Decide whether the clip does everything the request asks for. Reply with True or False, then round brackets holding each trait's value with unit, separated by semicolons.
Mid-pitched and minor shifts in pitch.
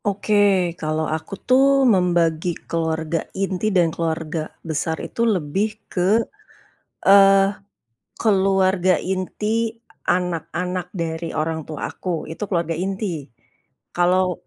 False (180 Hz; 3.2 semitones)